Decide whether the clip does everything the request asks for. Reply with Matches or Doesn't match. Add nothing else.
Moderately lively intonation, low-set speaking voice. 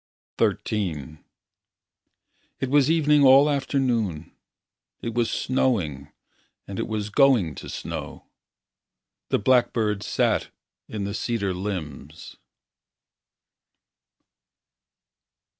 Doesn't match